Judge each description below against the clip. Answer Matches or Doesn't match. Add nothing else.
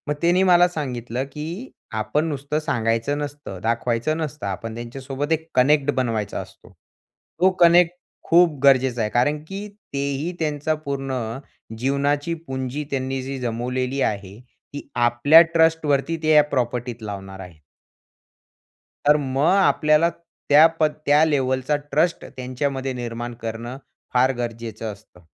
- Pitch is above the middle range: Doesn't match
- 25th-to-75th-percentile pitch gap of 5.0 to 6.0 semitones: Doesn't match